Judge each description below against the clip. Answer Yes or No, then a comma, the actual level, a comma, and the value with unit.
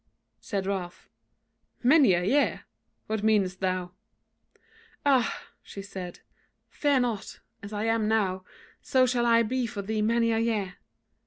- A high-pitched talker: Yes, high, 220 Hz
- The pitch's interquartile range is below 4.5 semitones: Yes, average, 3.4 semitones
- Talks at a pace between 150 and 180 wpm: No, average, 140 wpm